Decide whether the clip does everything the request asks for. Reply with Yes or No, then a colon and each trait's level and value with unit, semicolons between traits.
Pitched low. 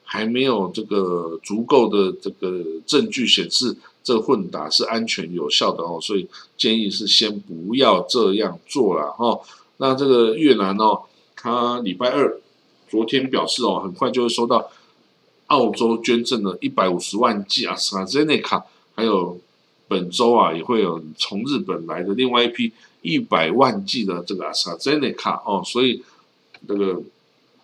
Yes: low, 115 Hz